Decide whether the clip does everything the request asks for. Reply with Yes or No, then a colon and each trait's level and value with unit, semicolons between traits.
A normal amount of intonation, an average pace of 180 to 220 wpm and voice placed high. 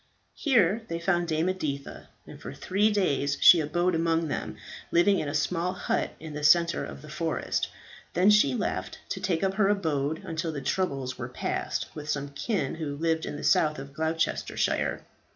No: average, 4.1 semitones; average, 185 wpm; medium, 160 Hz